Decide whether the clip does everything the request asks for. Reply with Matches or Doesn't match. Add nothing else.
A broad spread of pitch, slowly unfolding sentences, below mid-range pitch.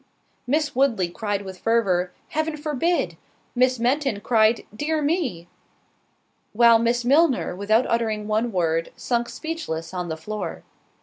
Doesn't match